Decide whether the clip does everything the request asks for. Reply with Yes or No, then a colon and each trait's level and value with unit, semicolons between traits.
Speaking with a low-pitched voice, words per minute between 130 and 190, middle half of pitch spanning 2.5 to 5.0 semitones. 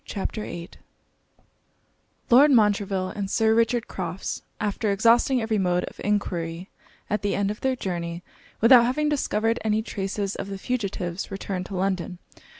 No: high, 205 Hz; average, 150 wpm; average, 3.3 semitones